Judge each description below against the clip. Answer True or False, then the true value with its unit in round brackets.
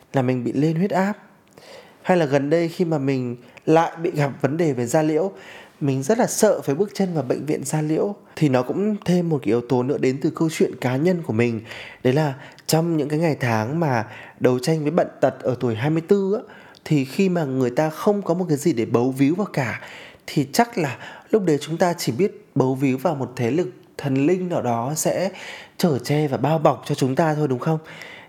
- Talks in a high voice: False (155 Hz)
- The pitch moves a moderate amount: True (4.9 semitones)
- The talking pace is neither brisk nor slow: True (240 wpm)